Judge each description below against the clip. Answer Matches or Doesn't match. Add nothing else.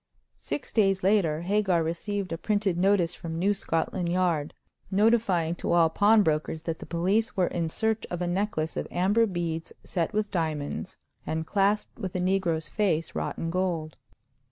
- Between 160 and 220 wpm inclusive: Matches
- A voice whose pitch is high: Doesn't match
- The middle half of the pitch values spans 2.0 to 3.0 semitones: Doesn't match